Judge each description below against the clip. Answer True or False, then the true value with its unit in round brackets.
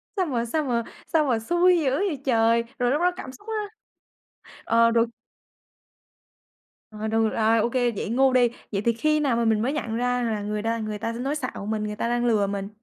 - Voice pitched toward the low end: False (235 Hz)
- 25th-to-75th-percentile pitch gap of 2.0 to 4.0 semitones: True (3.3 semitones)